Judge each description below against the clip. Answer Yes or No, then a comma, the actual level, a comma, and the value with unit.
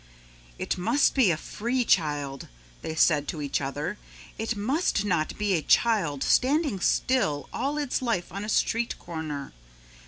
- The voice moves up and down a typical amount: No, wide, 7.4 semitones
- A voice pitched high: Yes, high, 195 Hz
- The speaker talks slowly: No, average, 155 wpm